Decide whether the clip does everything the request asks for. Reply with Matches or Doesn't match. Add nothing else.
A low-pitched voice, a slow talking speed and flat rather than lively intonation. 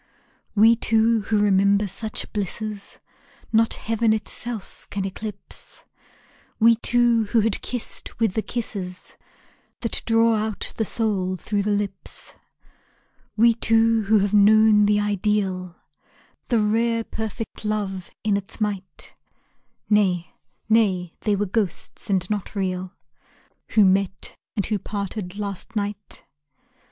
Doesn't match